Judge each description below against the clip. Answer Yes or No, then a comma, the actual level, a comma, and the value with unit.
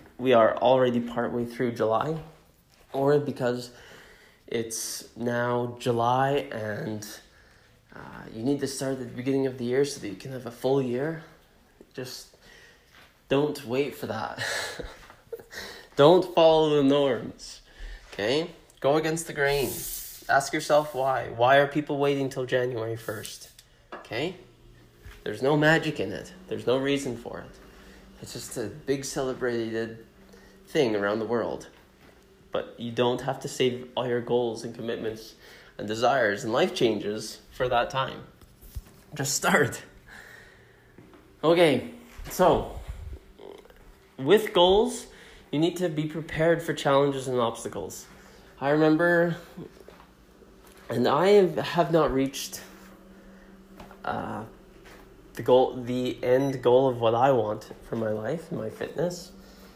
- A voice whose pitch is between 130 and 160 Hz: Yes, low, 135 Hz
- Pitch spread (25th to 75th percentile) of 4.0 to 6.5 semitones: Yes, average, 4.3 semitones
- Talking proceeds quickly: No, slow, 135 wpm